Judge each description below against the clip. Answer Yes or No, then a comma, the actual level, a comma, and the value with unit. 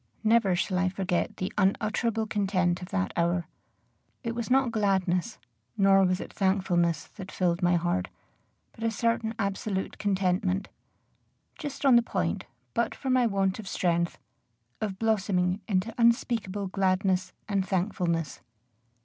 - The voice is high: Yes, high, 195 Hz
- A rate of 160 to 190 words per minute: No, average, 140 wpm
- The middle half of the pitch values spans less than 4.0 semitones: Yes, average, 3.4 semitones